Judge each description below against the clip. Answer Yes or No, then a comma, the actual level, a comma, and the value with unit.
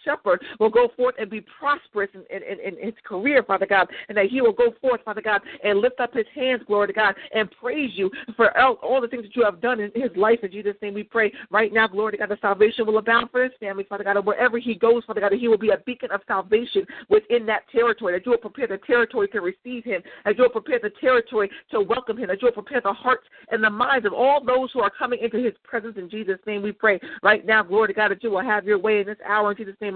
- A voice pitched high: Yes, high, 220 Hz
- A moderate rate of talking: No, fast, 280 wpm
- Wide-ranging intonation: No, average, 3.2 semitones